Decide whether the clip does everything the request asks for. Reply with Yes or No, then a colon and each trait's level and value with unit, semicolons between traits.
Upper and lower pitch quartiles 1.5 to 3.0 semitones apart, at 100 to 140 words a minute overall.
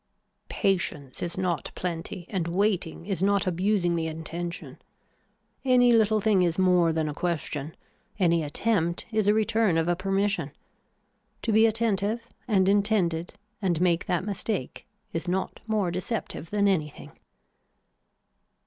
No: average, 3.5 semitones; slow, 135 wpm